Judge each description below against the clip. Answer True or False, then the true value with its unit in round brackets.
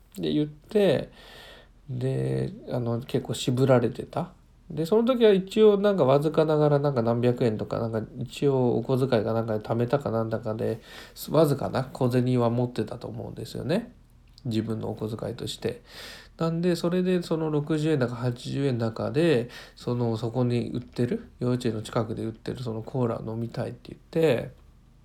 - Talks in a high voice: False (125 Hz)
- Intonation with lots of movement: False (4.8 semitones)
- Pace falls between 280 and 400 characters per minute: True (325 characters per minute)